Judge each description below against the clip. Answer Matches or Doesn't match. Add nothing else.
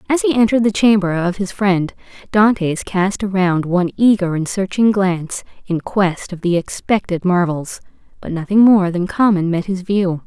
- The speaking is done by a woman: Matches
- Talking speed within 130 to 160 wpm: Doesn't match